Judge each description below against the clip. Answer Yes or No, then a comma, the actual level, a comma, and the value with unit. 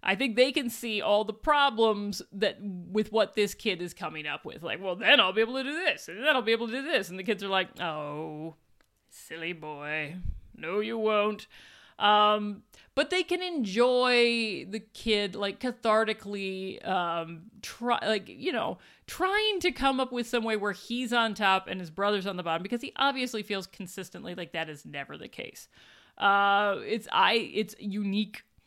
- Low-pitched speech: No, high, 210 Hz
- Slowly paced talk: No, average, 195 wpm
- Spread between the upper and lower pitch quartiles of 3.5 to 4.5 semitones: Yes, average, 4.0 semitones